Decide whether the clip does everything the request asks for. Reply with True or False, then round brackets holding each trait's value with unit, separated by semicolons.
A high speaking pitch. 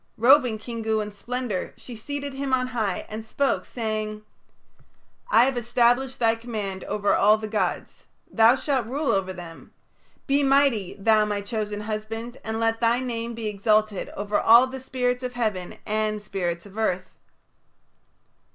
True (225 Hz)